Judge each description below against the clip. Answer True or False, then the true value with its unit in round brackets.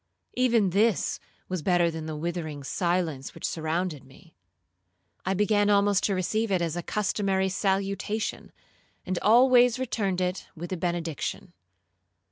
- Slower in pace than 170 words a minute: True (135 wpm)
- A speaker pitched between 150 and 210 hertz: True (185 Hz)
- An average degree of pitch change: True (3.3 semitones)